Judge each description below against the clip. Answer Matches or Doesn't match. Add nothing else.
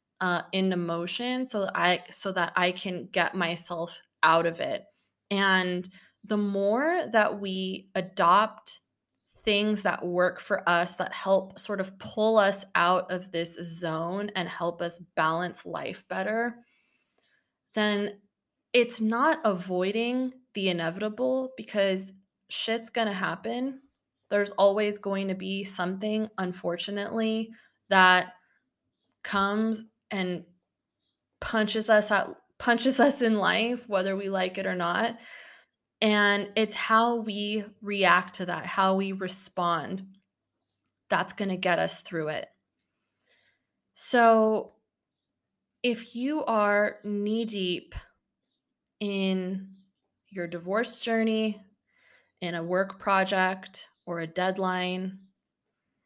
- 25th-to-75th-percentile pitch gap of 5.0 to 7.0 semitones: Doesn't match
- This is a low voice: Doesn't match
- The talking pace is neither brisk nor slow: Doesn't match